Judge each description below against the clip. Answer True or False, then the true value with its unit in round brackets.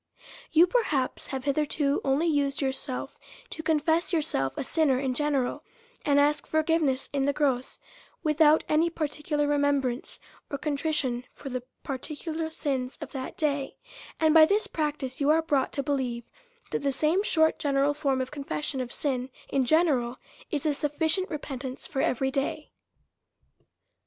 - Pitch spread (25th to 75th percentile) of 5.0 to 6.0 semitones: False (2.7 semitones)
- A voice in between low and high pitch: False (285 Hz)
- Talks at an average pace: True (155 wpm)